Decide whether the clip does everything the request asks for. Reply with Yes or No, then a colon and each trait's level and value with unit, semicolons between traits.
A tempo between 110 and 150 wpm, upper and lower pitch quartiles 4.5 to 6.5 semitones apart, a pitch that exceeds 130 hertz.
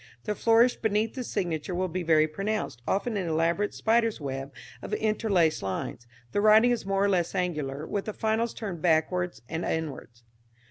No: average, 175 wpm; average, 5.3 semitones; medium, 185 Hz